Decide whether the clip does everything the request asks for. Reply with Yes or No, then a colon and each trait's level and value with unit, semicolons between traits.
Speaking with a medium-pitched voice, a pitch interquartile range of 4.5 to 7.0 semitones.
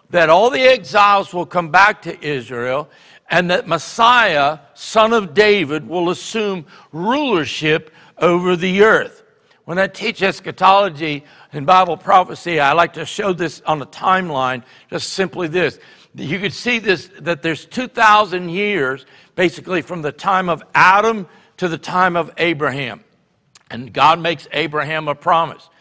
No: medium, 175 Hz; average, 4.1 semitones